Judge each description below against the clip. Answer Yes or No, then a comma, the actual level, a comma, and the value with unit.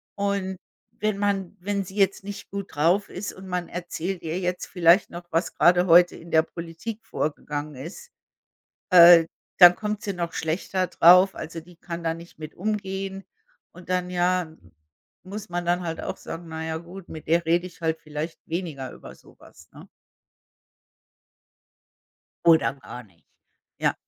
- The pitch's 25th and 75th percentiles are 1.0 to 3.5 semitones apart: Yes, average, 2.7 semitones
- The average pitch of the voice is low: No, medium, 175 Hz